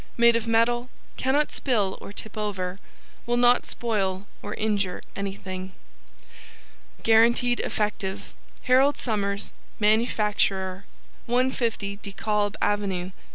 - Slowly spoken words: Yes, slow, 105 wpm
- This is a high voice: Yes, high, 210 Hz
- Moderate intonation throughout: Yes, average, 3.0 semitones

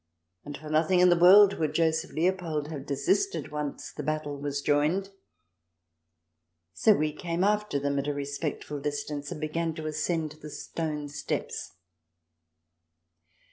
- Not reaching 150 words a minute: Yes, average, 140 wpm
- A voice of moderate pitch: Yes, medium, 155 Hz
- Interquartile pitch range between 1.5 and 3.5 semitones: Yes, average, 2.7 semitones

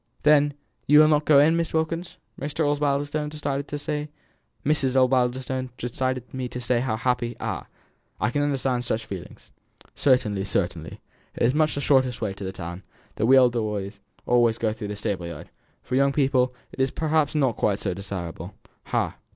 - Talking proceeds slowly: No, average, 170 wpm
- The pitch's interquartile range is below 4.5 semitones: No, average, 4.9 semitones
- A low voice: Yes, low, 130 Hz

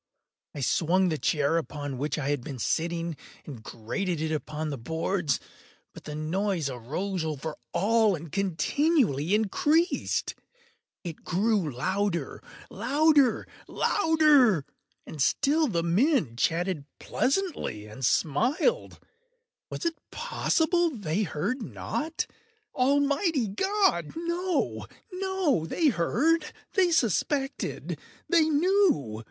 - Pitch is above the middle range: Yes, high, 195 Hz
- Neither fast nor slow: No, slow, 100 wpm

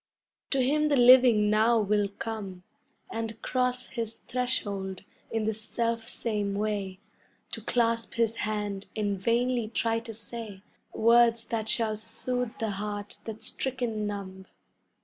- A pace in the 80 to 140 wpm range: Yes, slow, 135 wpm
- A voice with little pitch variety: Yes, narrow, 2.3 semitones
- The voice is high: Yes, high, 225 Hz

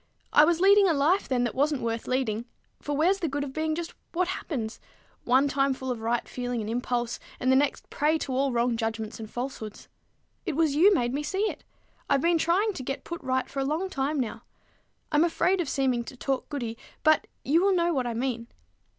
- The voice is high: Yes, very high, 275 Hz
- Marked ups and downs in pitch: No, average, 4.8 semitones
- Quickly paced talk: Yes, fast, 225 wpm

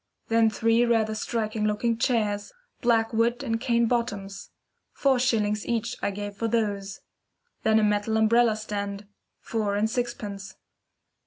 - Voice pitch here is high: Yes, high, 220 Hz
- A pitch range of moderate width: No, narrow, 2.2 semitones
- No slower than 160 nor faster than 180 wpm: No, average, 140 wpm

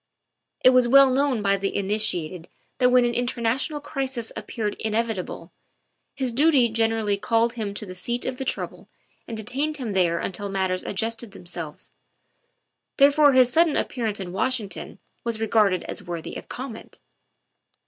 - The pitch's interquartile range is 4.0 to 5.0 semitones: Yes, average, 4.4 semitones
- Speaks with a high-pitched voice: Yes, high, 225 Hz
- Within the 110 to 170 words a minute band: Yes, average, 160 wpm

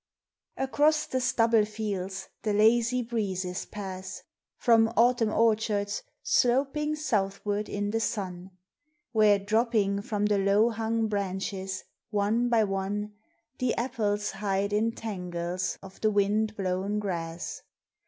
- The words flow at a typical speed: No, slow, 120 wpm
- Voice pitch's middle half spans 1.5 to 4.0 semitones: Yes, narrow, 2.6 semitones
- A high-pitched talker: Yes, high, 210 Hz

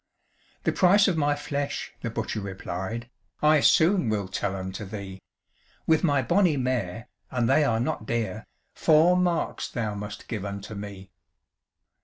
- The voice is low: Yes, low, 115 Hz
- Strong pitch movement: Yes, wide, 7.1 semitones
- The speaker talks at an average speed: Yes, average, 150 wpm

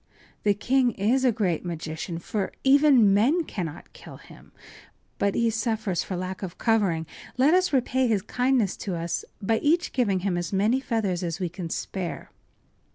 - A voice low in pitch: No, high, 205 Hz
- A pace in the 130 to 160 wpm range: No, average, 170 wpm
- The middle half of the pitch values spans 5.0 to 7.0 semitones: Yes, wide, 5.6 semitones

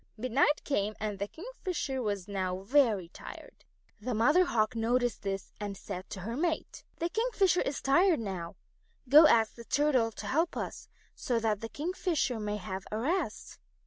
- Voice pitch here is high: Yes, high, 235 Hz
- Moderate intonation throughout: No, wide, 6.6 semitones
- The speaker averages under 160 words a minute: No, average, 175 wpm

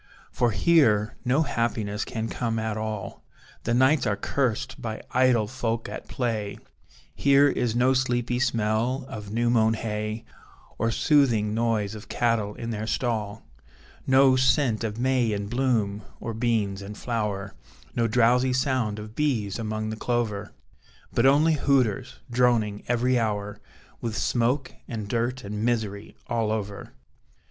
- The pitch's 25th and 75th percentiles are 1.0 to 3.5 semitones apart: Yes, average, 2.8 semitones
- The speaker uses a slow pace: No, average, 145 wpm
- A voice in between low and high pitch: No, low, 115 Hz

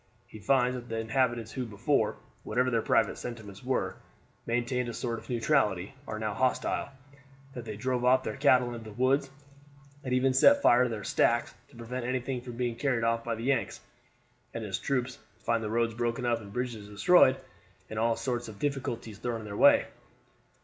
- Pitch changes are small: Yes, narrow, 2.2 semitones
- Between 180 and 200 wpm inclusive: Yes, average, 190 wpm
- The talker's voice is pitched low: Yes, low, 120 Hz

